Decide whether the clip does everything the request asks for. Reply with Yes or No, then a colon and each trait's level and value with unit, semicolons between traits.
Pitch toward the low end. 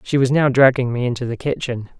Yes: low, 125 Hz